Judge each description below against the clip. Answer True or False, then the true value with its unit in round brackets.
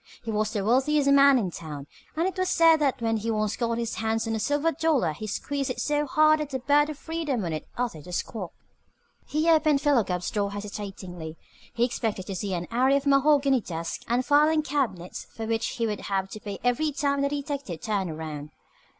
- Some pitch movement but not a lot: False (6.2 semitones)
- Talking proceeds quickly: True (215 wpm)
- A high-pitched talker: True (240 Hz)